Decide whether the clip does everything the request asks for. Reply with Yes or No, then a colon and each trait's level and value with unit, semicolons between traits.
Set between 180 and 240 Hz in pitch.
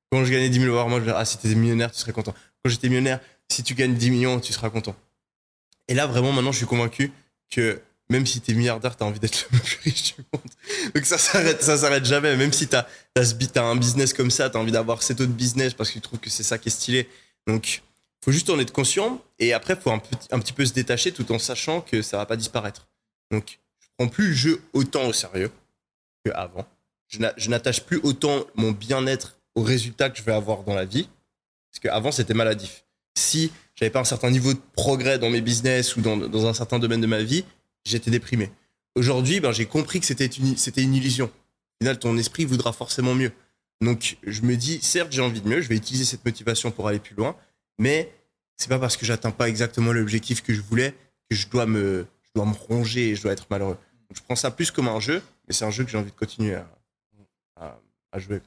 No: low, 120 Hz